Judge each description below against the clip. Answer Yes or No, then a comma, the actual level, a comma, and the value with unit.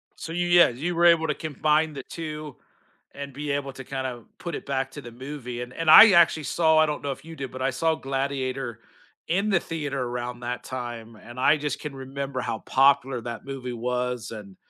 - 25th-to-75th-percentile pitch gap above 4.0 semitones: No, average, 3.7 semitones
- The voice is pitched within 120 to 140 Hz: Yes, low, 135 Hz